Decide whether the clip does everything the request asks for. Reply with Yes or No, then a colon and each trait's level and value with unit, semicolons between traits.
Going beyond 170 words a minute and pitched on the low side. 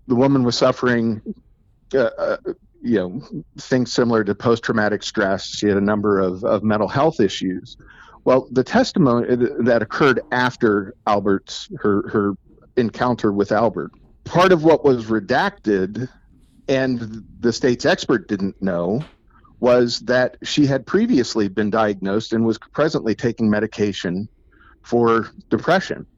No: slow, 135 wpm; low, 120 Hz